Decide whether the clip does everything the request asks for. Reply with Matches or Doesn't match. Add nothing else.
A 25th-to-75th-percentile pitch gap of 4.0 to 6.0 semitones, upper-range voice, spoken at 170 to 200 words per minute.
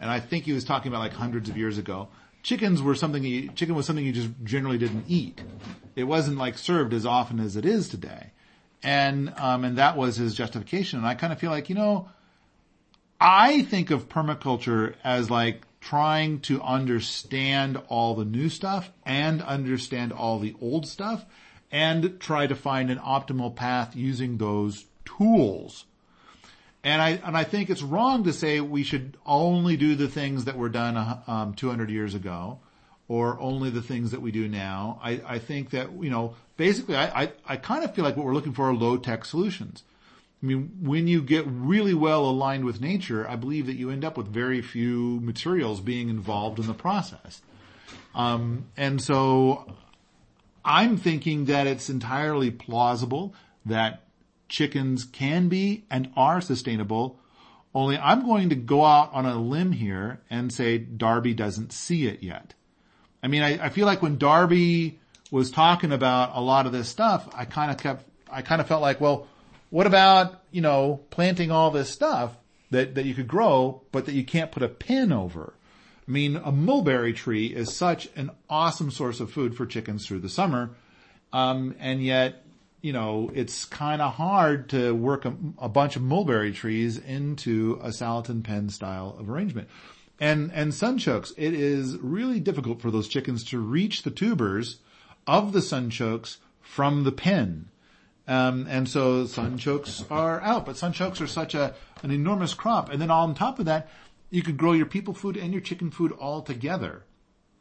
Doesn't match